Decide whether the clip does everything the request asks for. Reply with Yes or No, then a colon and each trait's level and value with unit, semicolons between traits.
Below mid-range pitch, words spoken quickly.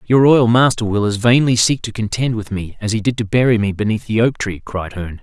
Yes: low, 110 Hz; fast, 265 wpm